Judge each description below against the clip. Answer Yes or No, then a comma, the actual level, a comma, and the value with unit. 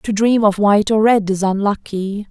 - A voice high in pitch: Yes, high, 205 Hz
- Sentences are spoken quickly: Yes, fast, 210 wpm